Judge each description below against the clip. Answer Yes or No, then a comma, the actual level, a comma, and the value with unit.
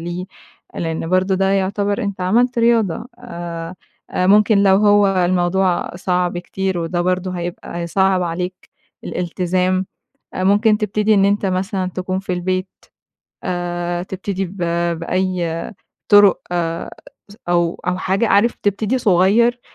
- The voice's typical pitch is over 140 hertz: Yes, medium, 185 Hz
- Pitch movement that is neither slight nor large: No, narrow, 2.3 semitones